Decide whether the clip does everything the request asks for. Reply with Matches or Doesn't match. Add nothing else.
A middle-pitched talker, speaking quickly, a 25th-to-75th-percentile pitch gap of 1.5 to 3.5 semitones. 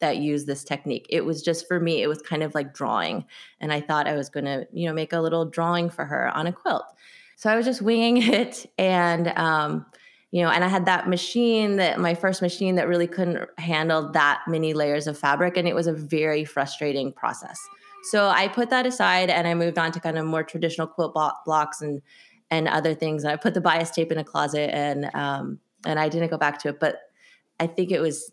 Matches